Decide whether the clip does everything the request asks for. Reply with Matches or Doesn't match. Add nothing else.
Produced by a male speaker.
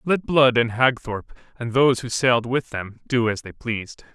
Matches